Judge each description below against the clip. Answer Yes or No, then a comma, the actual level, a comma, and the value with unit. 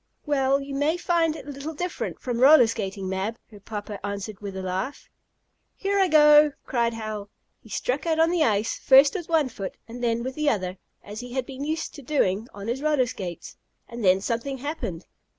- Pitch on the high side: Yes, very high, 250 Hz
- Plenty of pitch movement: Yes, wide, 6.3 semitones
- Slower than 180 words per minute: No, fast, 205 wpm